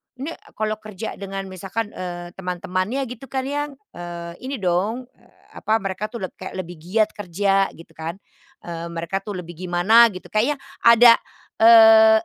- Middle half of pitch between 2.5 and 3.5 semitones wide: No, average, 4.3 semitones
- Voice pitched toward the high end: Yes, high, 195 Hz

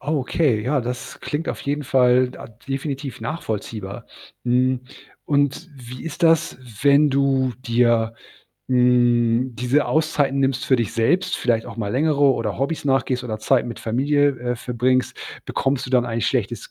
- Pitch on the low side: Yes, low, 130 Hz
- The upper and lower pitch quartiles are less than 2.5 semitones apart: No, average, 2.8 semitones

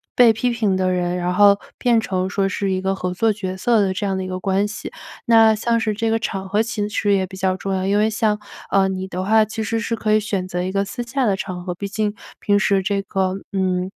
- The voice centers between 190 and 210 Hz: Yes, high, 200 Hz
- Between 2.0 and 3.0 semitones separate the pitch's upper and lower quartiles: Yes, narrow, 2.5 semitones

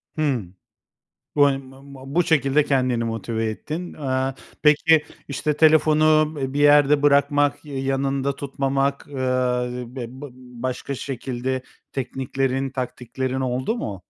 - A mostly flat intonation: Yes, narrow, 2.1 semitones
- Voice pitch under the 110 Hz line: No, low, 135 Hz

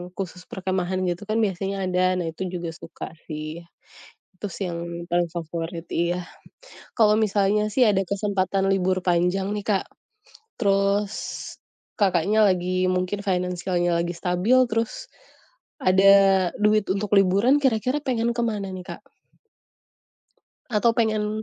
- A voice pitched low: No, high, 190 Hz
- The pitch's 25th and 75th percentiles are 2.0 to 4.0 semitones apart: Yes, average, 2.8 semitones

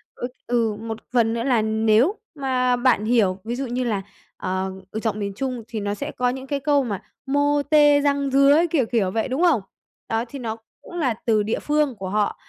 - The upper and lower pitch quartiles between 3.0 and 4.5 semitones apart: Yes, average, 4.0 semitones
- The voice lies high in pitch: Yes, high, 245 Hz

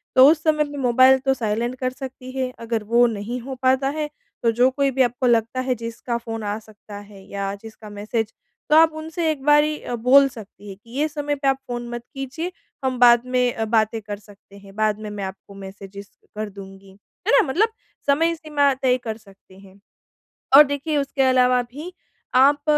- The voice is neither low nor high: No, high, 245 Hz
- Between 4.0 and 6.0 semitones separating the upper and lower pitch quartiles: Yes, average, 4.3 semitones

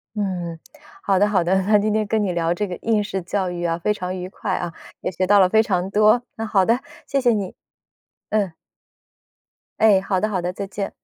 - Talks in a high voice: Yes, high, 195 Hz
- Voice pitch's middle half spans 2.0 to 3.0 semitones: Yes, narrow, 2.6 semitones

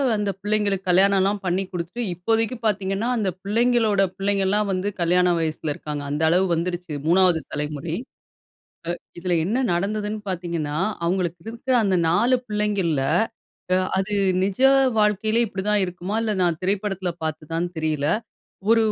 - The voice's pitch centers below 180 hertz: No, high, 190 Hz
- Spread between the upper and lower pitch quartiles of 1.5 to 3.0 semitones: No, average, 3.4 semitones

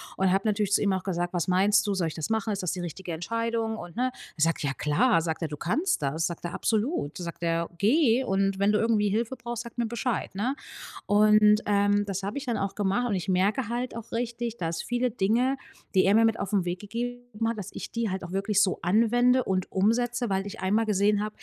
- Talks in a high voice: Yes, high, 205 Hz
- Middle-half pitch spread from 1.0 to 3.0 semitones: No, average, 3.7 semitones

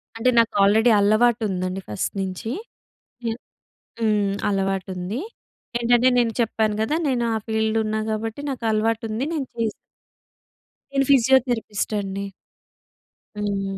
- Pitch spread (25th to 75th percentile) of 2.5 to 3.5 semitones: Yes, average, 2.9 semitones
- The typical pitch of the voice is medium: No, high, 220 Hz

